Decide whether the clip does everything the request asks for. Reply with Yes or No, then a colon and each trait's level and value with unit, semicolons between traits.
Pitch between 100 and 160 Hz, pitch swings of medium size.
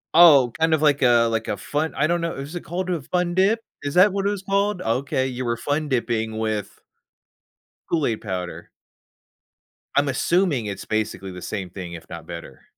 No: low, 135 Hz; wide, 7.8 semitones